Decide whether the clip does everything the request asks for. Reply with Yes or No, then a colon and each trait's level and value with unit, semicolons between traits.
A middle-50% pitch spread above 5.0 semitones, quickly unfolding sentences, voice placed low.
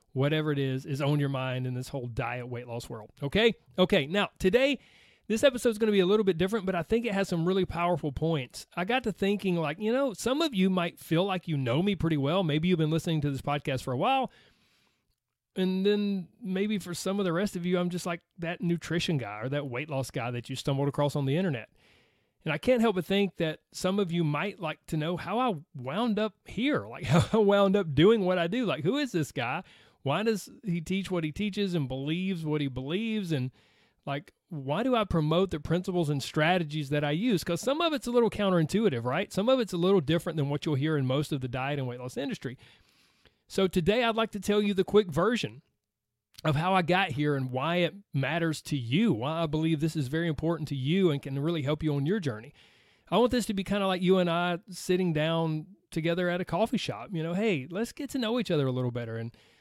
No: wide, 5.4 semitones; fast, 250 wpm; medium, 170 Hz